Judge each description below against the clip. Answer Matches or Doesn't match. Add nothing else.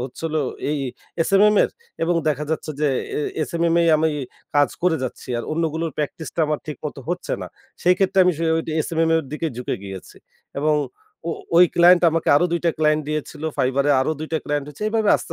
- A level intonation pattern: Matches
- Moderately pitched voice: Matches